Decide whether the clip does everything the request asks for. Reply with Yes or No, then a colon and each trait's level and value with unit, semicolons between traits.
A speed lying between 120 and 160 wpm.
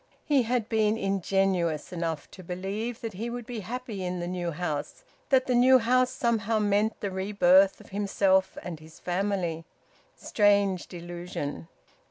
Yes: average, 155 wpm